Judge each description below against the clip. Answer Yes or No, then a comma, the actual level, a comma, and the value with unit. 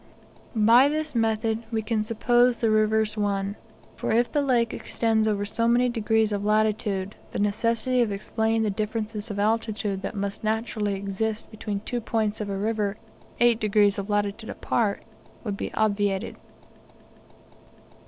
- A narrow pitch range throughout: Yes, narrow, 1.8 semitones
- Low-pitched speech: No, high, 215 Hz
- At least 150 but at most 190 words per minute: Yes, average, 155 wpm